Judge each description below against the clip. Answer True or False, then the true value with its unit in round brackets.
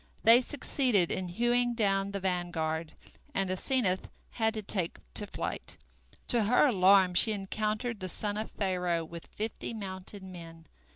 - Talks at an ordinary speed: True (150 wpm)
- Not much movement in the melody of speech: False (3.5 semitones)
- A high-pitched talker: True (195 Hz)